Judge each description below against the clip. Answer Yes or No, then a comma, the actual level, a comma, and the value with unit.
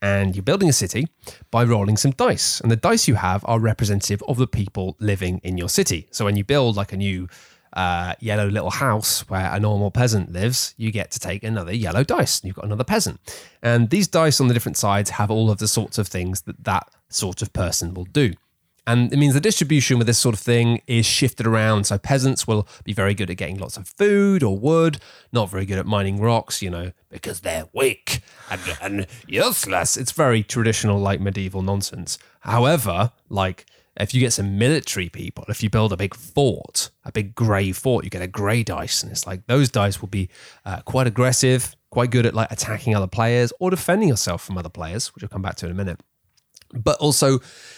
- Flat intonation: No, average, 4.1 semitones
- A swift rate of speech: Yes, fast, 220 wpm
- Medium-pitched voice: No, low, 110 Hz